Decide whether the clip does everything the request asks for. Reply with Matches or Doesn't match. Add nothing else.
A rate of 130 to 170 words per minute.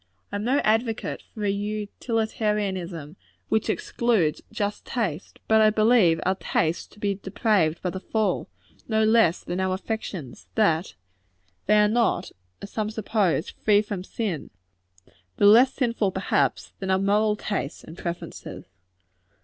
Matches